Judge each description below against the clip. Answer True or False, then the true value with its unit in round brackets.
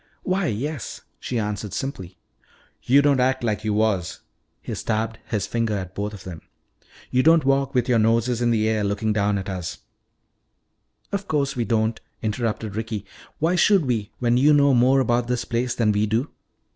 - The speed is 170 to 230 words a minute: True (185 wpm)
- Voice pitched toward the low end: True (115 Hz)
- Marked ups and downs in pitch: False (3.8 semitones)